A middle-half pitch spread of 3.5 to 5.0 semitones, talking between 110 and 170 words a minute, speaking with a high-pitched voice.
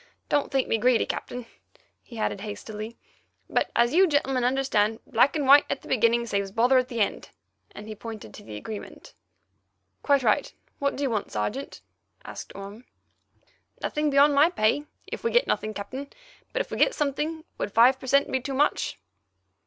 No: average, 4.5 semitones; average, 180 wpm; very high, 255 Hz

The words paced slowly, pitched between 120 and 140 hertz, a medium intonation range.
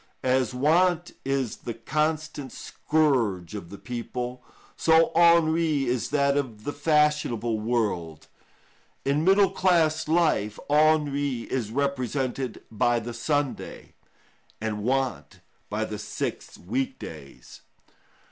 Yes: slow, 110 wpm; low, 135 Hz; average, 4.7 semitones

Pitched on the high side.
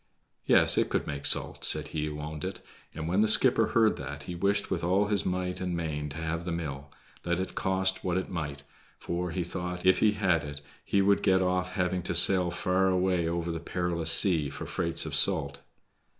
No: very low, 90 Hz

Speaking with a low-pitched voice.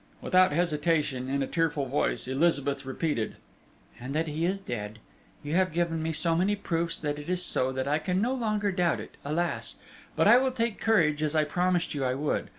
No: medium, 160 Hz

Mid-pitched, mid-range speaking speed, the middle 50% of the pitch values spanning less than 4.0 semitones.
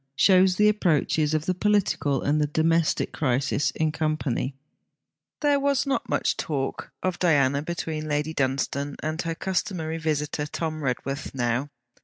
Yes: medium, 155 Hz; average, 145 wpm; average, 3.3 semitones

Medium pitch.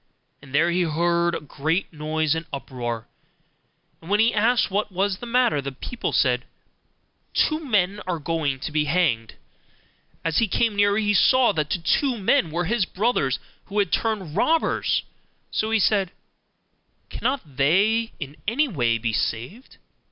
Yes: medium, 180 Hz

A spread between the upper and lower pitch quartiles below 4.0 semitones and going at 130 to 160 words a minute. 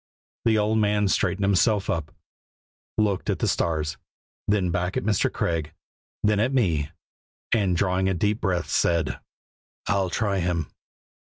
Yes: average, 3.3 semitones; average, 150 wpm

